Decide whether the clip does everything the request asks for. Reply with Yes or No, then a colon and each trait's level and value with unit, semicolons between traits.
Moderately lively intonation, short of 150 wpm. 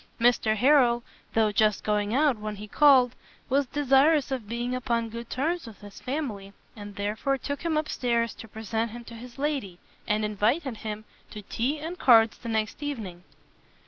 No: average, 4.2 semitones; average, 175 wpm